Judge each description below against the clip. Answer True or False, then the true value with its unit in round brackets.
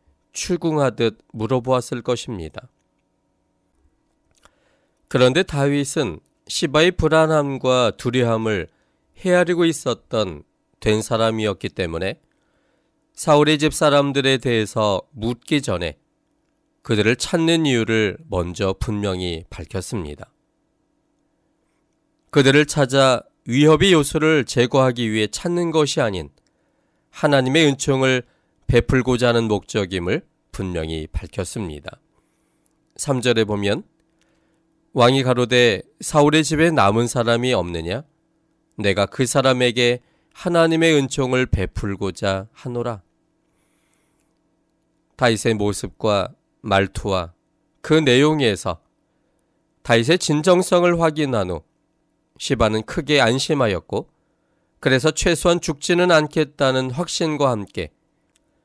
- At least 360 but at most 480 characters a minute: False (230 characters per minute)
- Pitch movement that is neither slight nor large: False (6.5 semitones)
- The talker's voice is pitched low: True (130 Hz)